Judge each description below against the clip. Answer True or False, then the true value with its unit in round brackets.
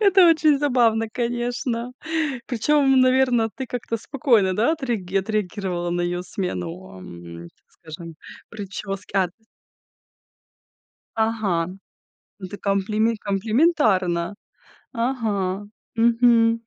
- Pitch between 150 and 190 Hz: False (220 Hz)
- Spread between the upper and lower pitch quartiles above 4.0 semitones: True (4.6 semitones)